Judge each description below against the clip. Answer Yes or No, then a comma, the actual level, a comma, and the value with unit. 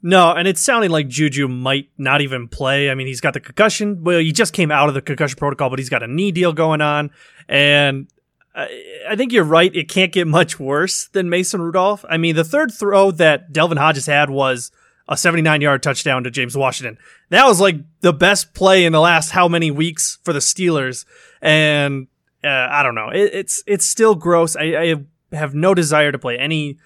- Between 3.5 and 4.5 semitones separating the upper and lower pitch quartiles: Yes, average, 4.1 semitones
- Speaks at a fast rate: Yes, fast, 215 wpm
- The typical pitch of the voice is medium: Yes, medium, 160 Hz